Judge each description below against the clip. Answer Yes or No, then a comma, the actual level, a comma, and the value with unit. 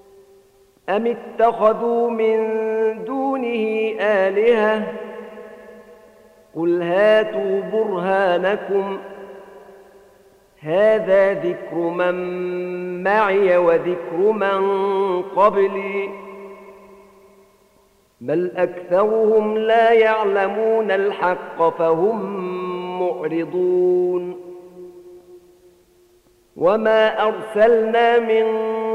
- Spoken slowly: Yes, slow, 55 wpm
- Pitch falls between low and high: No, high, 200 Hz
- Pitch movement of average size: Yes, average, 3.3 semitones